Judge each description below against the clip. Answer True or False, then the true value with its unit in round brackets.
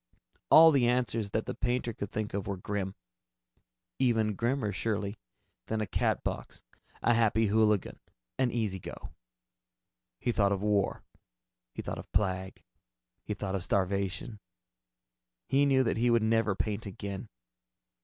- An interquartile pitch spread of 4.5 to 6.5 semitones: False (2.8 semitones)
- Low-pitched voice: True (110 Hz)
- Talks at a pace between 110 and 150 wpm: True (145 wpm)